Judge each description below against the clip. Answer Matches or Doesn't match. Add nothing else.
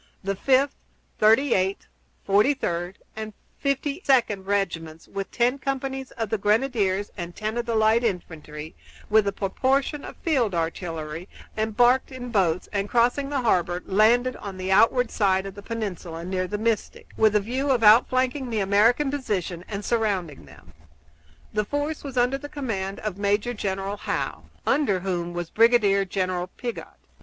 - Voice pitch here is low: Doesn't match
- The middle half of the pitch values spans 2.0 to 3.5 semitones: Doesn't match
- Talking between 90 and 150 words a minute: Doesn't match